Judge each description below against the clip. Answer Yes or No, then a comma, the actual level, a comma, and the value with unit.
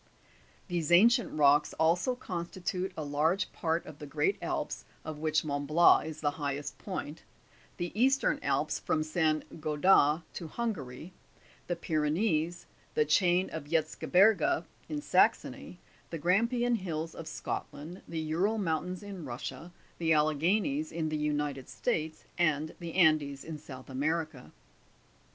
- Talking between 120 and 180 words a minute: Yes, average, 140 wpm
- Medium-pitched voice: Yes, medium, 160 Hz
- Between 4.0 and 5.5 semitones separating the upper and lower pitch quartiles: No, average, 3.4 semitones